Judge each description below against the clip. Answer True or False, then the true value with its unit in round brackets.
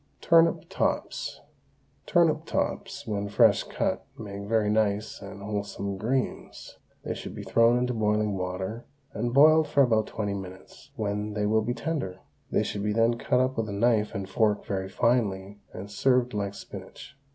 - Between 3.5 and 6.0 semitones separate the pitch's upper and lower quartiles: False (3.0 semitones)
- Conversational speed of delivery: True (165 wpm)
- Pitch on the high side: False (105 Hz)